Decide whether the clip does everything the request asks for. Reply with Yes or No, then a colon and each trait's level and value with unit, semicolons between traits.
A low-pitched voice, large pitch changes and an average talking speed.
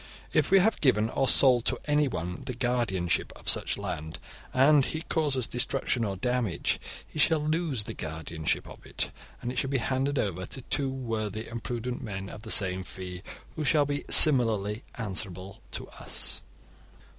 Yes: low, 120 Hz; wide, 5.7 semitones; average, 170 wpm